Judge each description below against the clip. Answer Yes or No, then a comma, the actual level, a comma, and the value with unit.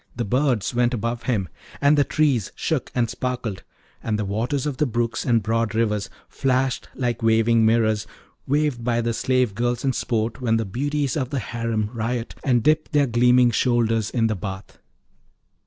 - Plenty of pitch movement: No, narrow, 2.4 semitones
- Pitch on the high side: No, low, 120 Hz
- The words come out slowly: No, average, 175 wpm